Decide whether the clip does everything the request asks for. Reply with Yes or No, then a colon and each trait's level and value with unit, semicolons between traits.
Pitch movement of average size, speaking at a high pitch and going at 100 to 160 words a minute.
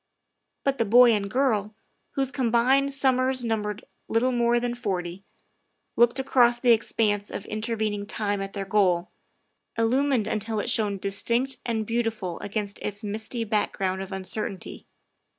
Yes: average, 3.0 semitones; high, 220 Hz; average, 150 wpm